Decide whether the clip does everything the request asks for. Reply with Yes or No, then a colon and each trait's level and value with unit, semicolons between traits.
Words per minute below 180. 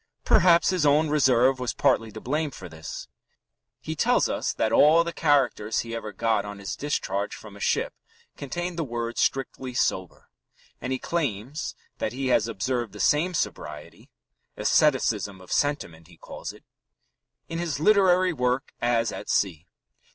Yes: average, 160 wpm